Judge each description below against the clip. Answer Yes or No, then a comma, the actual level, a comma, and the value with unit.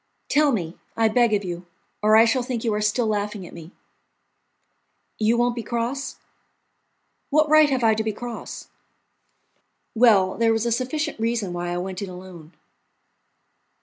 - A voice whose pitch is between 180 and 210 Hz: No, high, 225 Hz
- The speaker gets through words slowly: No, average, 165 wpm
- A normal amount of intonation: Yes, average, 3.9 semitones